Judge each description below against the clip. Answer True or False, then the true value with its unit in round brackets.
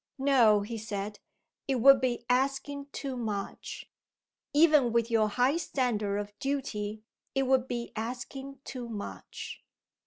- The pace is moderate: False (130 wpm)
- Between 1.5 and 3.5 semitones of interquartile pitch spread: False (4.0 semitones)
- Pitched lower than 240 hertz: False (245 Hz)